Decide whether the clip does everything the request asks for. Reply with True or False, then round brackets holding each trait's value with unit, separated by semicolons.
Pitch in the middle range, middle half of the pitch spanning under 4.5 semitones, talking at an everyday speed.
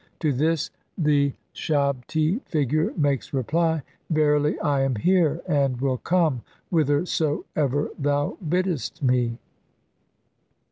False (145 Hz; 2.8 semitones; 100 wpm)